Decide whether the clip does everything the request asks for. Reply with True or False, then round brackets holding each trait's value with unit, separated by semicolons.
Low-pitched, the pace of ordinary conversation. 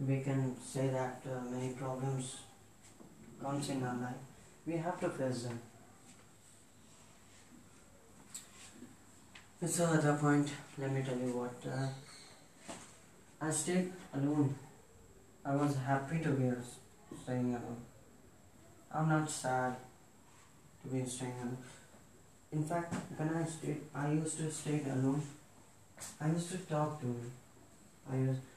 False (130 Hz; 130 wpm)